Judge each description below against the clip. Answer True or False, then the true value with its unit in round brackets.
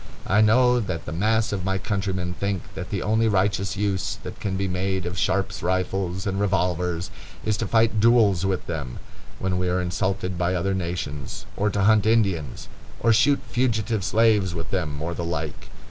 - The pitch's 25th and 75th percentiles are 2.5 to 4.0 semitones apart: True (2.9 semitones)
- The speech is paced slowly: False (185 wpm)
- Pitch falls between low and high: False (95 Hz)